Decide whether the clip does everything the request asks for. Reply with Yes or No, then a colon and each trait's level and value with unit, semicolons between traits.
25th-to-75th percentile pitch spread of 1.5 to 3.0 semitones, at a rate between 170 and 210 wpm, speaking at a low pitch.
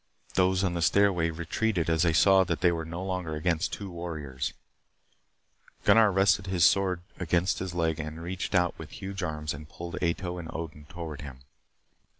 Yes: narrow, 2.6 semitones; average, 175 wpm; very low, 85 Hz